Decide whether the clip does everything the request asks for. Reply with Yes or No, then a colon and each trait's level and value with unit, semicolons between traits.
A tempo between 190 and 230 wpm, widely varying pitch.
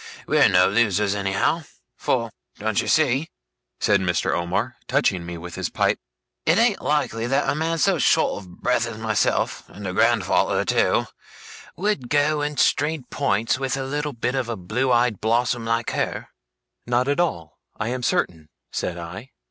No: average, 170 wpm; wide, 6.5 semitones